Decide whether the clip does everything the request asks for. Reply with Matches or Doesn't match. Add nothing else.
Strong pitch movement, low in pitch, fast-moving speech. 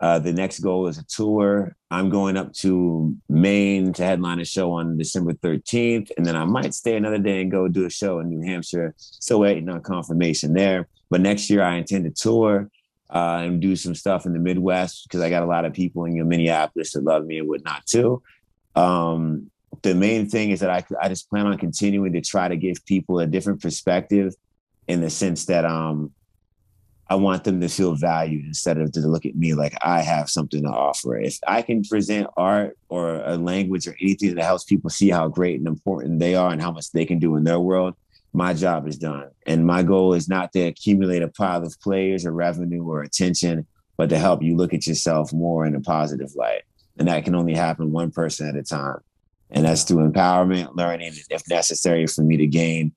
Doesn't match